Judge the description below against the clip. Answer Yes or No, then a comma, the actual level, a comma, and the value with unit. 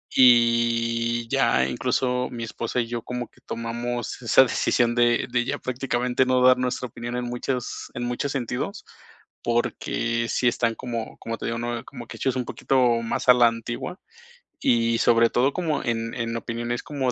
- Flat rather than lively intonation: Yes, narrow, 1.3 semitones